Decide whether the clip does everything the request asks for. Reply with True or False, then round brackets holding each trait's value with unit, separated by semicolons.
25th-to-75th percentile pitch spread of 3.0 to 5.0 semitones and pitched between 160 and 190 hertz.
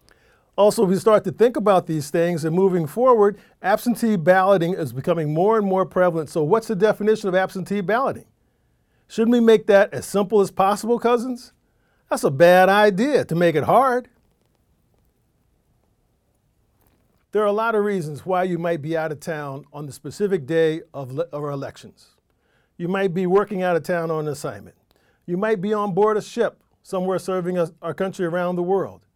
True (4.0 semitones; 185 Hz)